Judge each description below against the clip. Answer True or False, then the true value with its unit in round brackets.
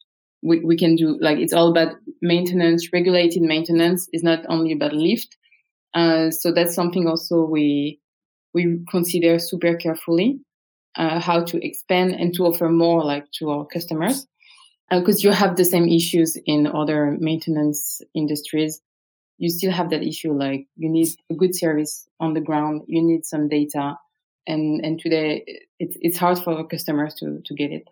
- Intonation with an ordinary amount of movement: False (2.1 semitones)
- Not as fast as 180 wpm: True (170 wpm)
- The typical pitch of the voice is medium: True (165 Hz)